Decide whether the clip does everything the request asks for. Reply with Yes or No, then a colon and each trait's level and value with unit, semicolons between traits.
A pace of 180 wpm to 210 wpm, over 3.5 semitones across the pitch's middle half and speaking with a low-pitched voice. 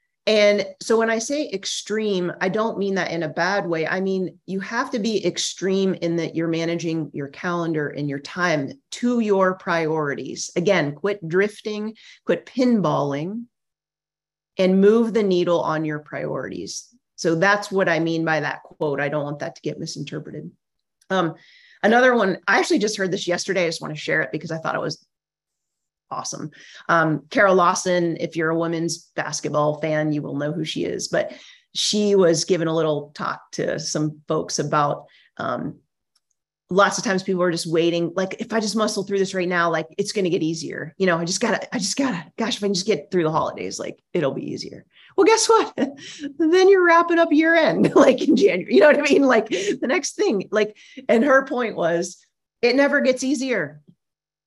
No: average, 200 wpm; average, 5.3 semitones; medium, 185 Hz